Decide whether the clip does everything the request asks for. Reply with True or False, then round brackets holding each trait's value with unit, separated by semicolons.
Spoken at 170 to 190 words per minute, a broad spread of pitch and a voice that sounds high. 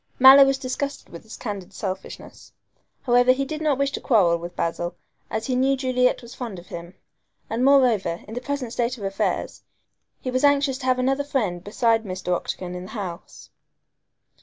True (185 wpm; 5.9 semitones; 240 Hz)